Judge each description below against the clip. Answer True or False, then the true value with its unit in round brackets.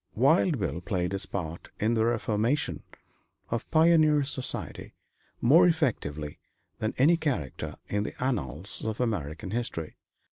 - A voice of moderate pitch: False (115 Hz)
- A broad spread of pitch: True (8.1 semitones)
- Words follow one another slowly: True (130 wpm)